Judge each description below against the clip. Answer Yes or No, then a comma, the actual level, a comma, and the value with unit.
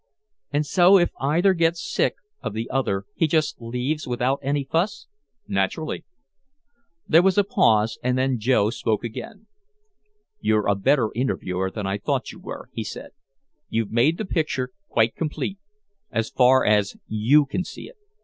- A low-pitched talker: Yes, low, 130 Hz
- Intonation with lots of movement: Yes, wide, 6.7 semitones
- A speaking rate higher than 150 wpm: Yes, average, 160 wpm